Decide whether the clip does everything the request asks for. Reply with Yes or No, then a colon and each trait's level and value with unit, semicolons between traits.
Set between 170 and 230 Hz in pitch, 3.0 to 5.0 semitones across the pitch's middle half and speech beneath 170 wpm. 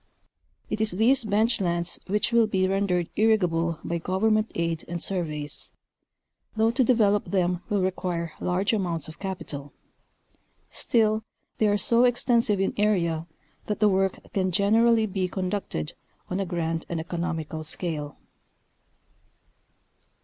Yes: high, 190 Hz; average, 4.0 semitones; slow, 135 wpm